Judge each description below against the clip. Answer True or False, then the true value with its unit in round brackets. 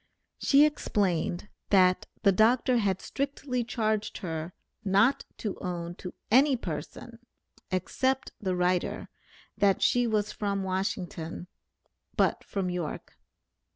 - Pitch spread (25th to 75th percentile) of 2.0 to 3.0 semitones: False (4.5 semitones)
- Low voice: False (200 Hz)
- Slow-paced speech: True (115 wpm)